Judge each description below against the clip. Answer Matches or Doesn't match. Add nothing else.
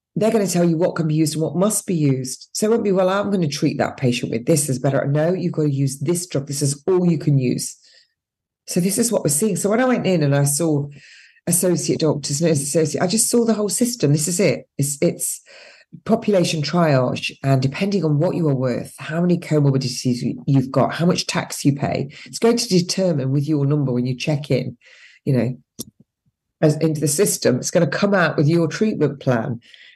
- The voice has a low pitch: Doesn't match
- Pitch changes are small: Doesn't match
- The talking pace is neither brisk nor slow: Doesn't match